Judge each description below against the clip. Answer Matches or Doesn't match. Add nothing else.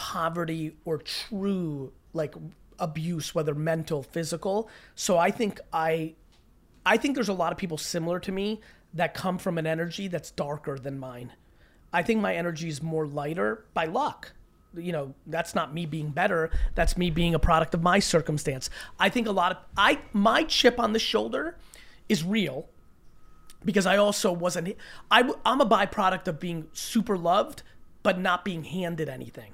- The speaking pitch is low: Doesn't match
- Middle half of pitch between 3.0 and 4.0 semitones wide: Matches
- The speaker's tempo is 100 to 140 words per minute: Doesn't match